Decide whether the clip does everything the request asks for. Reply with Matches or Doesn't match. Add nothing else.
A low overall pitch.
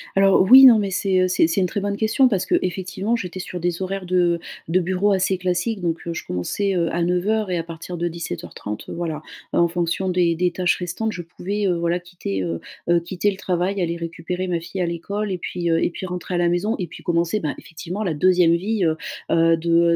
Doesn't match